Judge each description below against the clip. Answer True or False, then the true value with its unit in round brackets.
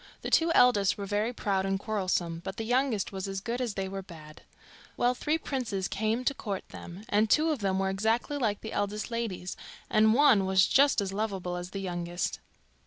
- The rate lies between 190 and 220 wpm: True (205 wpm)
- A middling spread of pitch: True (3.6 semitones)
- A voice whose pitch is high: True (205 Hz)